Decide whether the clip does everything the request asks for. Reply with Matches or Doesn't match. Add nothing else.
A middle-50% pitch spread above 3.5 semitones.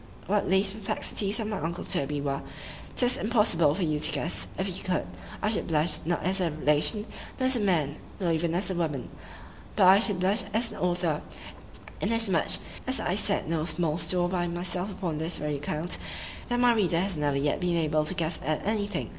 Matches